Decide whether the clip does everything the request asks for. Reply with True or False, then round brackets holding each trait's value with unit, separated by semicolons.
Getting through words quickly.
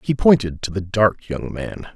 True (215 wpm)